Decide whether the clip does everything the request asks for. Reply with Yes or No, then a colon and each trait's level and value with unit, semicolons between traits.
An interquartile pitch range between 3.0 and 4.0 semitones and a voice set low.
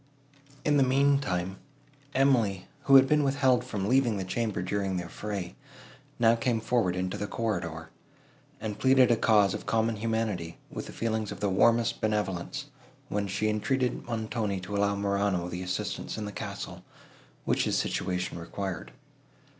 Yes: average, 3.7 semitones; low, 105 Hz